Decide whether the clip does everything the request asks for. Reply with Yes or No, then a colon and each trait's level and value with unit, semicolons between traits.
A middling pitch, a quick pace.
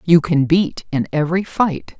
No: medium, 160 Hz; average, 180 wpm